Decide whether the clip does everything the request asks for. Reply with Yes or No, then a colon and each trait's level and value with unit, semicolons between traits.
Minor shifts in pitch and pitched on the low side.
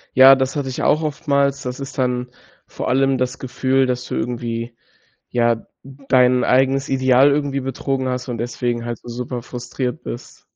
Yes: narrow, 1.7 semitones; low, 130 Hz